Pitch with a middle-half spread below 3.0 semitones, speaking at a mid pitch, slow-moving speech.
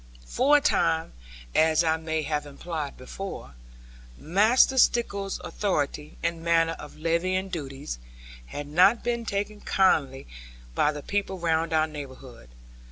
No: average, 4.8 semitones; medium, 165 Hz; slow, 130 wpm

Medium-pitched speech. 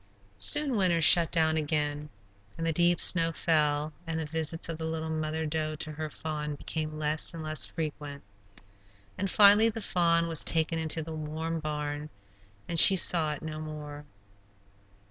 Yes: medium, 160 Hz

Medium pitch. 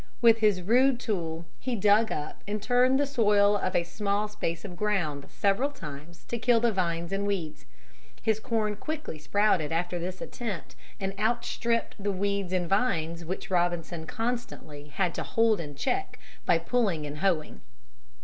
No: high, 200 Hz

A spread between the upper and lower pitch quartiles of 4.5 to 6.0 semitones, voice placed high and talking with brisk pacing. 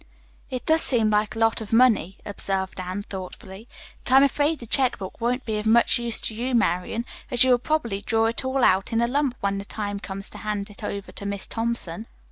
No: average, 3.5 semitones; high, 225 Hz; fast, 230 wpm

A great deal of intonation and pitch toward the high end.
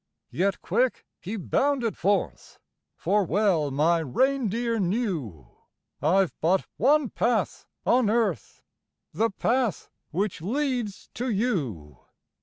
Yes: wide, 6.0 semitones; high, 205 Hz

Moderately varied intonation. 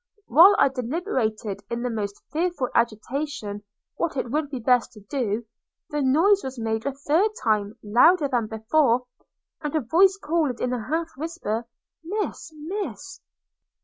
No: wide, 6.0 semitones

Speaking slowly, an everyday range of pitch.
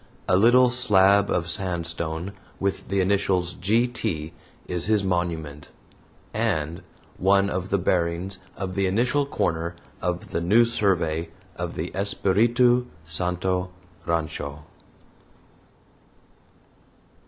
Yes: slow, 110 wpm; average, 3.0 semitones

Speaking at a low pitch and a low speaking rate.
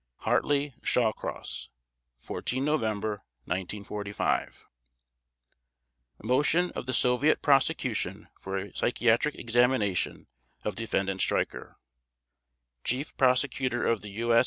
Yes: low, 120 Hz; slow, 95 wpm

